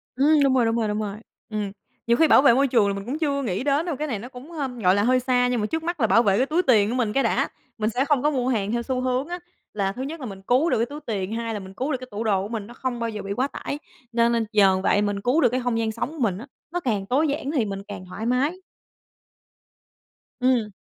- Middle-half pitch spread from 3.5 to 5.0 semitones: Yes, average, 4.5 semitones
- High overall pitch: Yes, high, 240 Hz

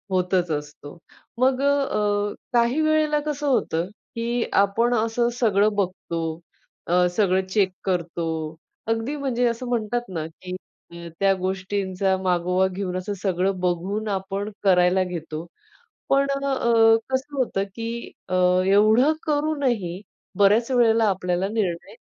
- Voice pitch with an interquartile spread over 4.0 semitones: Yes, average, 4.7 semitones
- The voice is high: Yes, high, 205 Hz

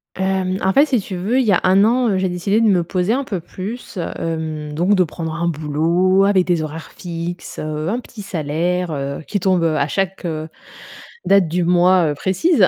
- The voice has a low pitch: No, medium, 180 Hz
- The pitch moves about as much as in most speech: Yes, average, 3.1 semitones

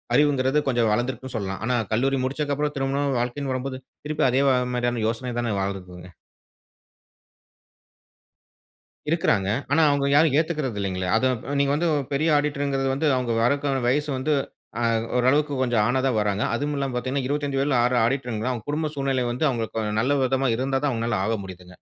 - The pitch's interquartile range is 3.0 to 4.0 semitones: Yes, average, 3.4 semitones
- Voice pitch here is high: No, low, 130 Hz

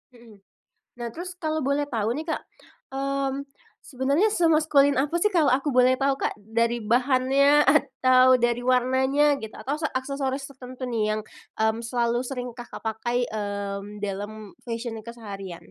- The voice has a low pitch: No, very high, 255 Hz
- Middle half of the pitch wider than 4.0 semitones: No, average, 3.3 semitones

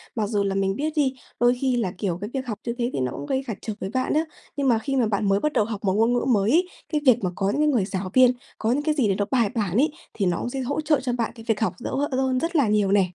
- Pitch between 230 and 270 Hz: Yes, high, 235 Hz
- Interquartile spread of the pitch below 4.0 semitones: No, average, 4.7 semitones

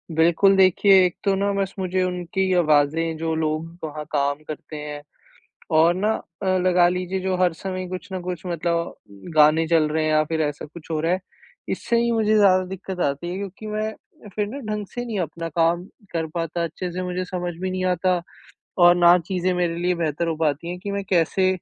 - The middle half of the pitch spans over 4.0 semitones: No, narrow, 2.5 semitones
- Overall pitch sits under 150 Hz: No, medium, 175 Hz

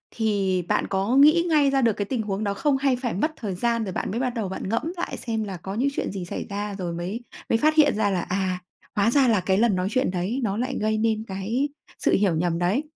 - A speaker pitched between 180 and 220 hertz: Yes, high, 215 Hz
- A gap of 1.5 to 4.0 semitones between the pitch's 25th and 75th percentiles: No, average, 4.8 semitones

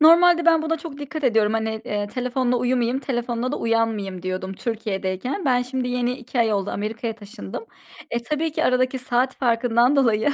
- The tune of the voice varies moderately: Yes, average, 3.1 semitones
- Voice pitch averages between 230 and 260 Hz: Yes, high, 245 Hz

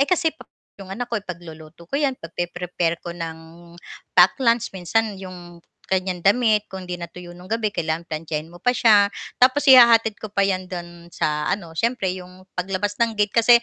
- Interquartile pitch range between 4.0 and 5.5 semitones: Yes, average, 4.5 semitones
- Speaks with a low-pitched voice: No, medium, 185 Hz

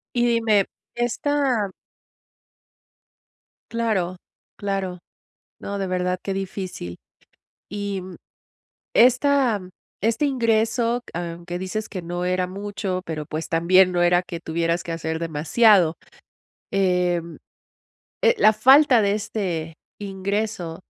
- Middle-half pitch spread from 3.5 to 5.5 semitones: Yes, average, 4.0 semitones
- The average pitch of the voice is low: No, high, 190 Hz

